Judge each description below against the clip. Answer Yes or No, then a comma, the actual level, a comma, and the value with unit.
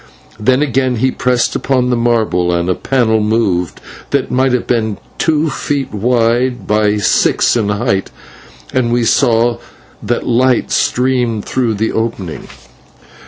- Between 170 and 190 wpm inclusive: No, average, 140 wpm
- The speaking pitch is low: Yes, low, 120 Hz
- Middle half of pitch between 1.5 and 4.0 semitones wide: Yes, average, 2.9 semitones